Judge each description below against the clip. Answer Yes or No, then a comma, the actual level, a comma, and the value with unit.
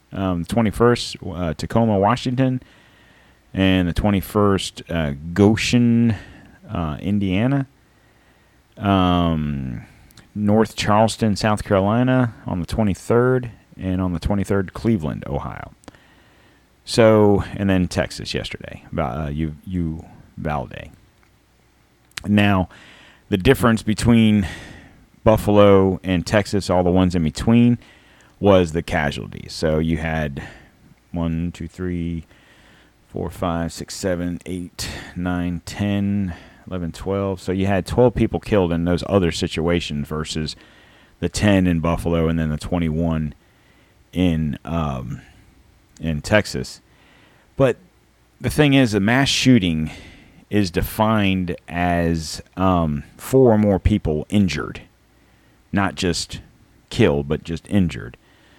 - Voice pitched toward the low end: Yes, very low, 95 Hz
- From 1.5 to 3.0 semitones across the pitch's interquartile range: No, average, 3.8 semitones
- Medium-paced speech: No, slow, 115 wpm